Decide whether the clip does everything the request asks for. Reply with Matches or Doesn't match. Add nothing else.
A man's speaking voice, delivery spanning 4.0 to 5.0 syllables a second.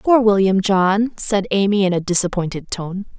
Doesn't match